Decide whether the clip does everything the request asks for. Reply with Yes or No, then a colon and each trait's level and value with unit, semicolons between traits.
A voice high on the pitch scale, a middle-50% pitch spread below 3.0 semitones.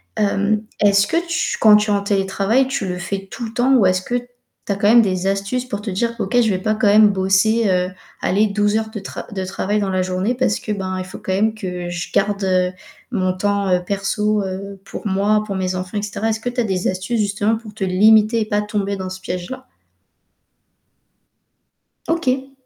Yes: high, 205 Hz; narrow, 2.5 semitones